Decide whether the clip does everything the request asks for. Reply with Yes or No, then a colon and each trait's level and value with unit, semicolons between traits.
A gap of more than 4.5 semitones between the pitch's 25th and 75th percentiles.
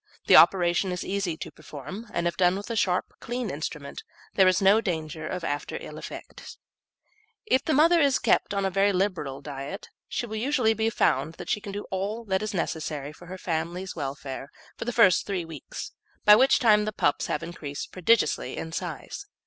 Yes: average, 4.9 semitones